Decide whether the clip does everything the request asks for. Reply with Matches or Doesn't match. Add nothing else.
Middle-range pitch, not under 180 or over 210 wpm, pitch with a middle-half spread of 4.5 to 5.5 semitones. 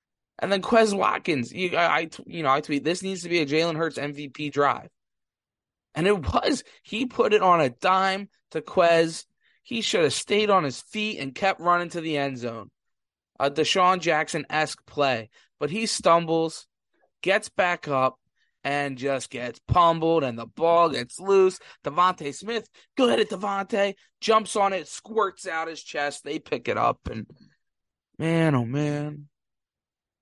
Doesn't match